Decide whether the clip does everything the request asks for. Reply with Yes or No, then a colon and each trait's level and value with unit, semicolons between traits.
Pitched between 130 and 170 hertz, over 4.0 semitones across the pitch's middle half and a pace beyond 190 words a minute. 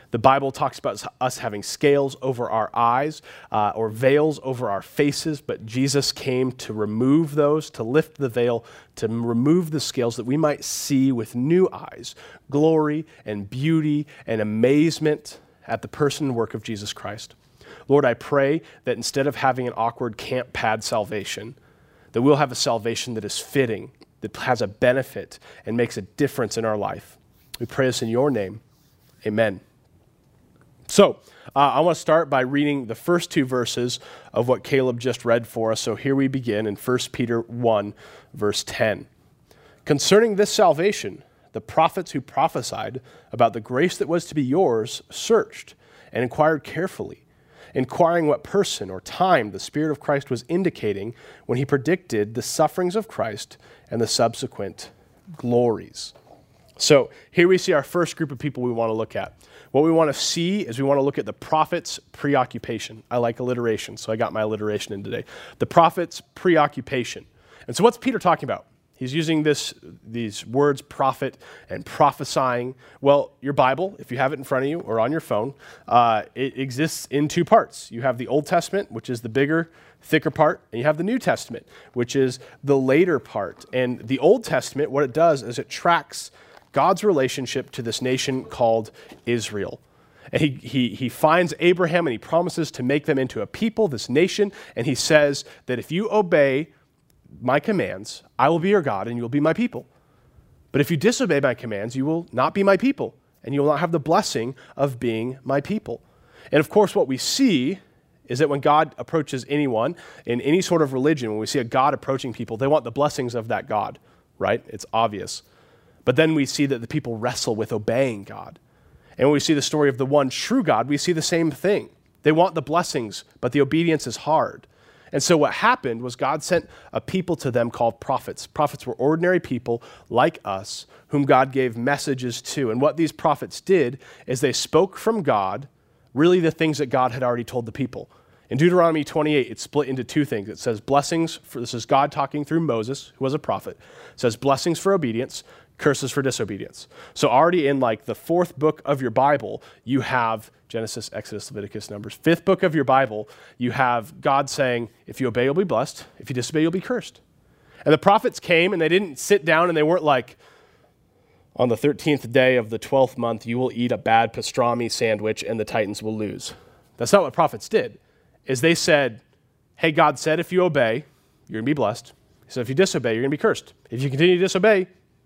Yes: low, 135 Hz; average, 4.6 semitones; average, 200 wpm